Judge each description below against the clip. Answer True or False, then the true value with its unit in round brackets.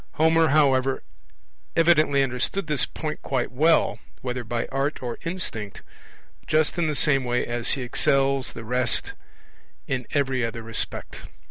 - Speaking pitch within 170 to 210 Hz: False (135 Hz)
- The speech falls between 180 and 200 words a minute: False (140 wpm)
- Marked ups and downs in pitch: False (3.8 semitones)